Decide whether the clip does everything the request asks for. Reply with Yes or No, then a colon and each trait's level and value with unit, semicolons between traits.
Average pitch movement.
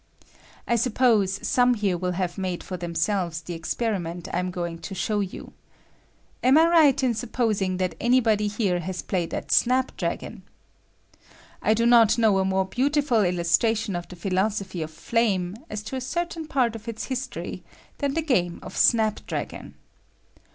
Yes: average, 5.0 semitones